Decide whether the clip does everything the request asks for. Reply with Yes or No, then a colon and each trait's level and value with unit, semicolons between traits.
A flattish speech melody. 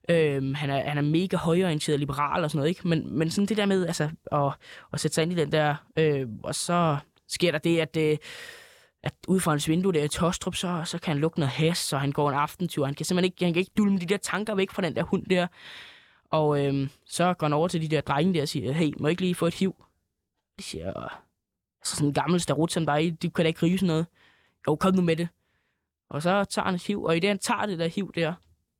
No: average, 3.5 semitones